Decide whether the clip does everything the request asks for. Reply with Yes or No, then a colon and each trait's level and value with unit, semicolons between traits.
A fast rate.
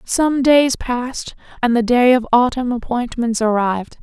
No: average, 150 wpm